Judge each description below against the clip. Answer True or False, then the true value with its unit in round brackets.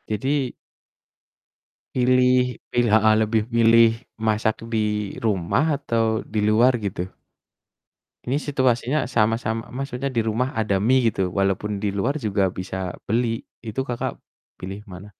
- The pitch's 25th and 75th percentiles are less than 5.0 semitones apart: True (3.3 semitones)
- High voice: False (115 Hz)